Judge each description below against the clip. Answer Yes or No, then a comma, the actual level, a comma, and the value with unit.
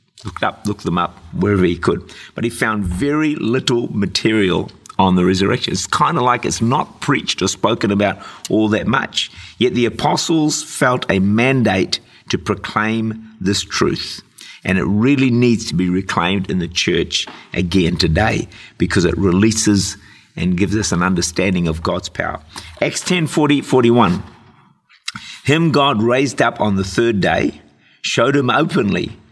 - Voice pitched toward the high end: No, low, 110 Hz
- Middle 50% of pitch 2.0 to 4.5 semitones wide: No, average, 4.9 semitones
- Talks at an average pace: Yes, average, 160 wpm